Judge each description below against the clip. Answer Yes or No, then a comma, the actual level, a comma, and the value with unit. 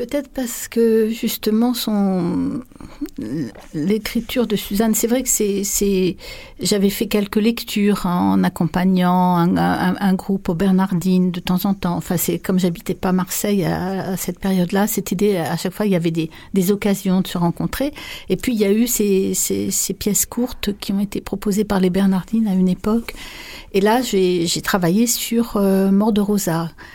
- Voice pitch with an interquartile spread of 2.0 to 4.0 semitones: Yes, average, 3.2 semitones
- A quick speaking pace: No, average, 190 wpm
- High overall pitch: Yes, high, 200 Hz